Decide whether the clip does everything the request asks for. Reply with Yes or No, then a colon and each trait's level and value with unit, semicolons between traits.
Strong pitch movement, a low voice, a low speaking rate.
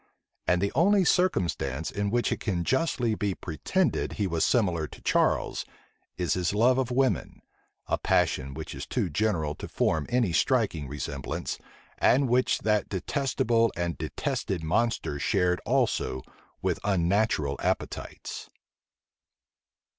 Yes: wide, 6.7 semitones; low, 100 Hz; slow, 130 wpm